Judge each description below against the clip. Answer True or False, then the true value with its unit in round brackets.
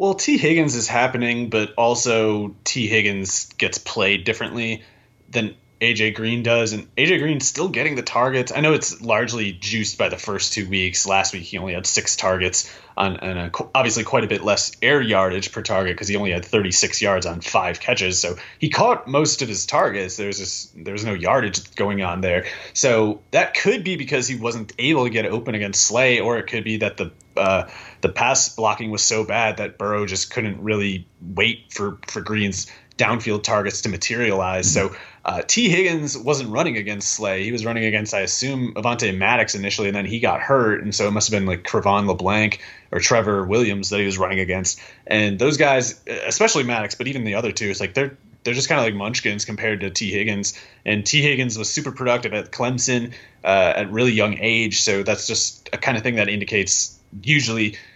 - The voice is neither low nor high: False (110 Hz)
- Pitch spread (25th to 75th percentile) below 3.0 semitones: False (3.4 semitones)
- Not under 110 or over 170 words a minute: False (205 wpm)